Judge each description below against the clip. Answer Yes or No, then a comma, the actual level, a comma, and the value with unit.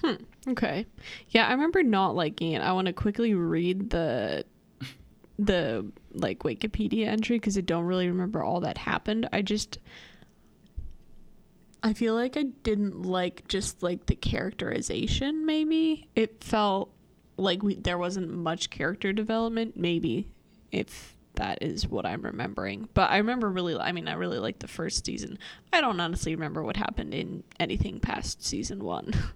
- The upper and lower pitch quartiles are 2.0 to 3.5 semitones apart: No, average, 4.3 semitones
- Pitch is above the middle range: Yes, high, 200 Hz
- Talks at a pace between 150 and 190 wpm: Yes, average, 160 wpm